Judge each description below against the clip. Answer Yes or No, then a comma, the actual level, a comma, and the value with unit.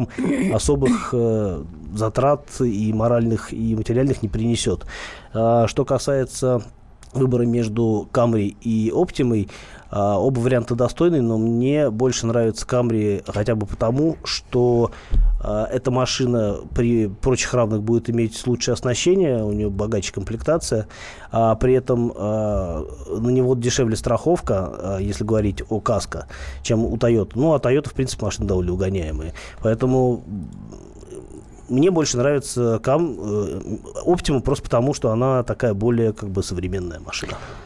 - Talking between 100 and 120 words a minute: No, average, 135 wpm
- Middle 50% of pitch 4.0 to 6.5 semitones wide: No, average, 3.4 semitones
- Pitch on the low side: Yes, low, 115 Hz